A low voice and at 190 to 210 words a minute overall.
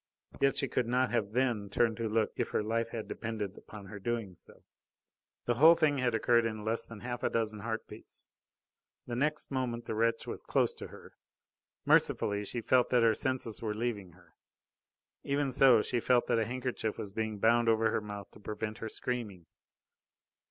Yes: low, 115 Hz; average, 195 wpm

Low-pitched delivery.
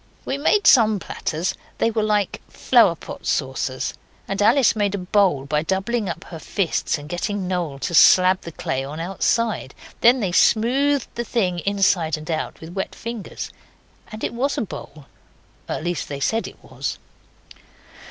No: high, 190 Hz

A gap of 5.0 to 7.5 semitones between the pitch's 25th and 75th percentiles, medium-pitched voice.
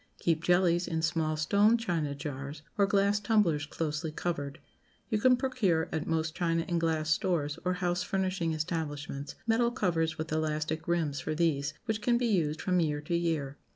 No: average, 3.3 semitones; medium, 165 Hz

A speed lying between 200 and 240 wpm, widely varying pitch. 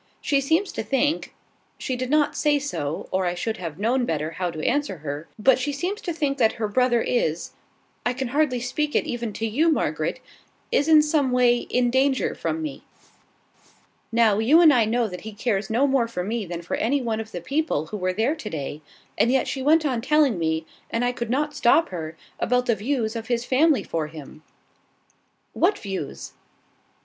Yes: fast, 205 wpm; wide, 5.8 semitones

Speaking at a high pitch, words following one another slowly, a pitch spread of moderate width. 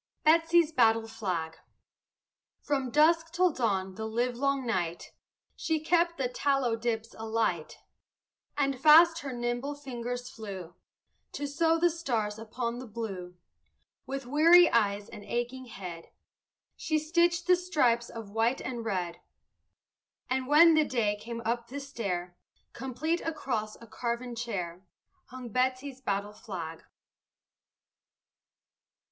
Yes: high, 245 Hz; slow, 125 wpm; average, 4.8 semitones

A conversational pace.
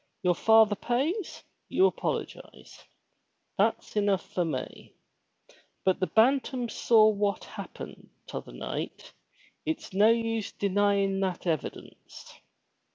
No: slow, 115 wpm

